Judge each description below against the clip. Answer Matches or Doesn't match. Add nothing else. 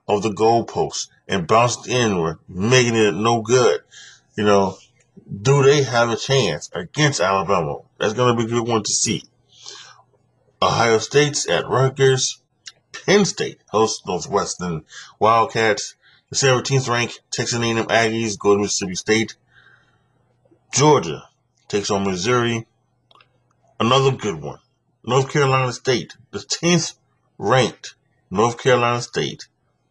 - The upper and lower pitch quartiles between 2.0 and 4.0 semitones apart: Matches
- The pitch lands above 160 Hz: Doesn't match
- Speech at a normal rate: Doesn't match